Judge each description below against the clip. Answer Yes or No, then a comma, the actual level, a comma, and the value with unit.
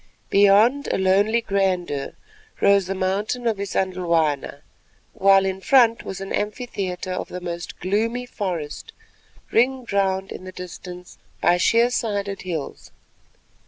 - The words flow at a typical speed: No, slow, 125 wpm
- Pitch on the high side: Yes, high, 195 Hz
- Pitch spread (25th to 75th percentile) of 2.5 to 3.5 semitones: Yes, average, 2.9 semitones